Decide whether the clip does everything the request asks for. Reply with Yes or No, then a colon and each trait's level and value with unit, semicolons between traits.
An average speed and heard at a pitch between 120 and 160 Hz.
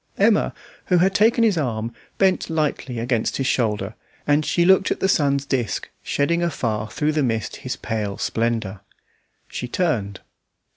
Yes: average, 155 wpm; medium, 140 Hz